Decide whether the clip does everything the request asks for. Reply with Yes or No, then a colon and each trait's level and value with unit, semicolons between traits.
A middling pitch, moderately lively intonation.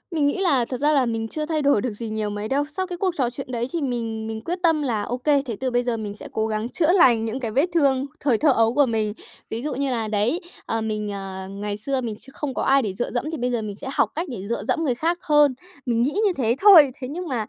No: very high, 250 Hz; average, 4.9 semitones